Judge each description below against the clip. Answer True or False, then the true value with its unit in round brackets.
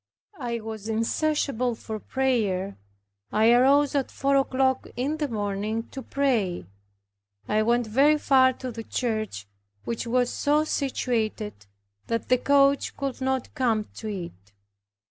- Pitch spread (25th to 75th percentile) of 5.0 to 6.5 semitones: False (3.8 semitones)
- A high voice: True (245 Hz)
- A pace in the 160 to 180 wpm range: False (135 wpm)